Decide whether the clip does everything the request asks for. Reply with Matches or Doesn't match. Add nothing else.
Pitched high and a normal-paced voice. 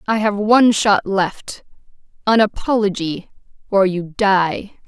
Doesn't match